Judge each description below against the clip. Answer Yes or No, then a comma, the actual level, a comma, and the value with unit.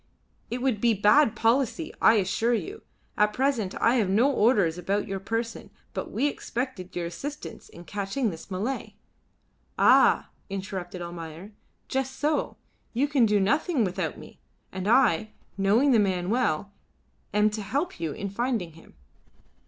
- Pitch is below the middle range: No, high, 215 Hz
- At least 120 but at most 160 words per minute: Yes, average, 150 wpm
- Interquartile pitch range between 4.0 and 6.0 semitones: Yes, average, 5.2 semitones